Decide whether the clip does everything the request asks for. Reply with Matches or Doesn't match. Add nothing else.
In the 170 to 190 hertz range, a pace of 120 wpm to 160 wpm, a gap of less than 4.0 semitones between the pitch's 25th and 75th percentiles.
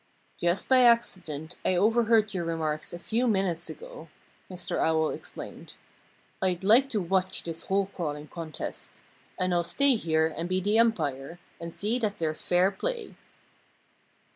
Doesn't match